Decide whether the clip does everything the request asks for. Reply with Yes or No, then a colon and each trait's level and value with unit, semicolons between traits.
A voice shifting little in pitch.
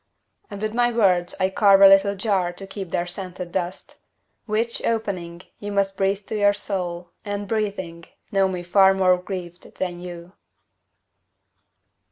Yes: narrow, 2.3 semitones